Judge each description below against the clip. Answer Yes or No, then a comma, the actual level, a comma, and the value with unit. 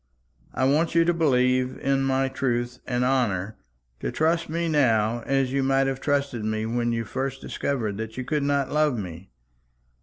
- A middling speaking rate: Yes, average, 180 wpm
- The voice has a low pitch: Yes, low, 130 Hz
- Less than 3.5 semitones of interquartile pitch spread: Yes, average, 3.0 semitones